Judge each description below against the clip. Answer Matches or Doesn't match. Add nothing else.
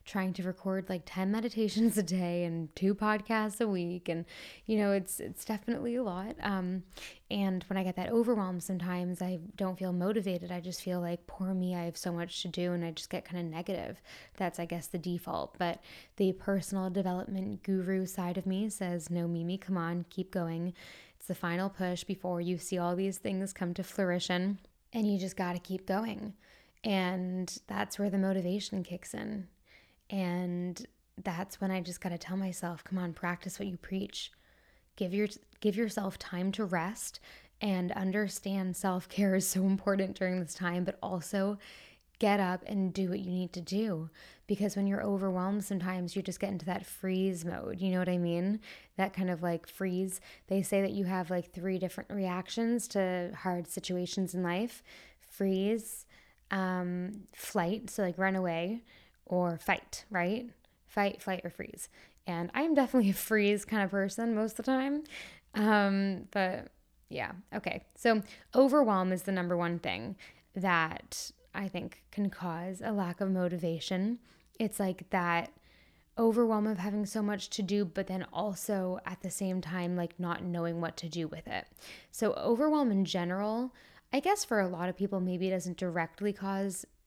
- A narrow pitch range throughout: Matches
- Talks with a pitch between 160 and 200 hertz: Matches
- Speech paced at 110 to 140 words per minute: Doesn't match